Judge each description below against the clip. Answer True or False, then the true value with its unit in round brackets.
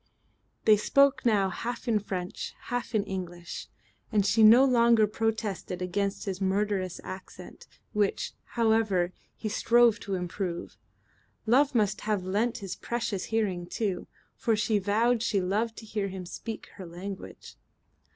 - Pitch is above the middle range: True (210 Hz)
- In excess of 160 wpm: False (140 wpm)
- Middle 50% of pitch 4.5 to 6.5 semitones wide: False (3.1 semitones)